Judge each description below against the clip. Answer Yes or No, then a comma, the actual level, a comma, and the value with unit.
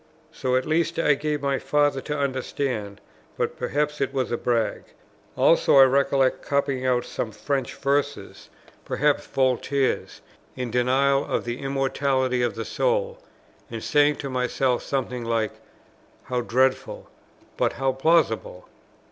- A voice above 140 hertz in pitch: No, low, 135 Hz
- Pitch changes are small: Yes, narrow, 2.3 semitones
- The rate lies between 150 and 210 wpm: No, average, 140 wpm